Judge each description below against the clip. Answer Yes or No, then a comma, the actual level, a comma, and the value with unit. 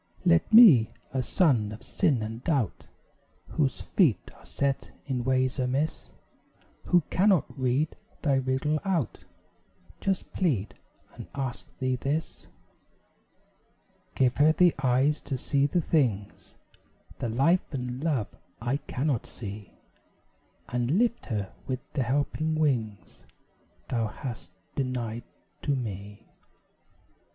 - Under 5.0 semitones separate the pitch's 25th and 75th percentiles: Yes, average, 4.2 semitones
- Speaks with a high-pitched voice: No, low, 130 Hz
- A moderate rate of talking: No, slow, 120 wpm